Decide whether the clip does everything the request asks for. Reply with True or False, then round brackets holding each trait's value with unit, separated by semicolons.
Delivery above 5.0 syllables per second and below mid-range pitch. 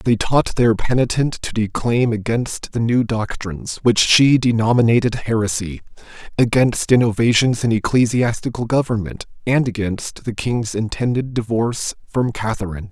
False (4.8 syllables/s; 115 Hz)